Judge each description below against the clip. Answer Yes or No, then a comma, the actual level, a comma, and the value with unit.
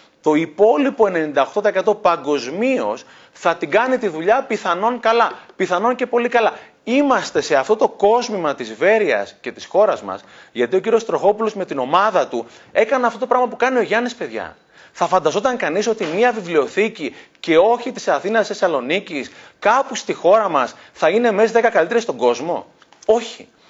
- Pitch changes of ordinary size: Yes, average, 4.3 semitones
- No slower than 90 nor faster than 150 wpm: No, average, 165 wpm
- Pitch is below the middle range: No, high, 220 Hz